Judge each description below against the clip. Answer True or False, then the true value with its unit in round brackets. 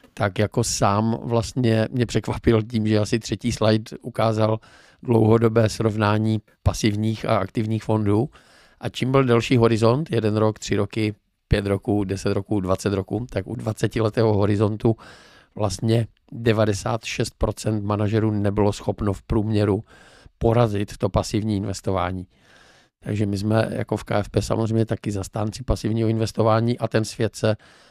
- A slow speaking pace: False (135 wpm)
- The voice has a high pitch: False (110 Hz)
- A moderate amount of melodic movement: False (1.8 semitones)